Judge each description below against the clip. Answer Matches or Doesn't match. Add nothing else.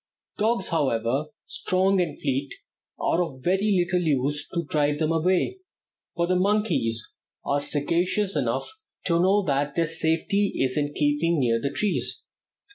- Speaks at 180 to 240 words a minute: Doesn't match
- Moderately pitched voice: Matches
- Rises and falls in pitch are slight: Doesn't match